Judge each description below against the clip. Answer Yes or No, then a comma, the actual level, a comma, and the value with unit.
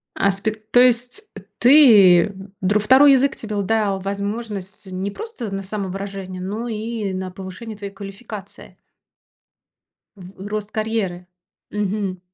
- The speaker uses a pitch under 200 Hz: No, high, 205 Hz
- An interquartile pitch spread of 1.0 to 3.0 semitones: Yes, narrow, 2.5 semitones